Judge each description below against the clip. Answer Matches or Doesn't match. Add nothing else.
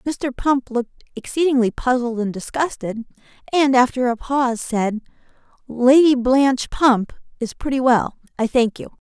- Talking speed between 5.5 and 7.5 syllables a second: Doesn't match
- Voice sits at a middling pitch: Doesn't match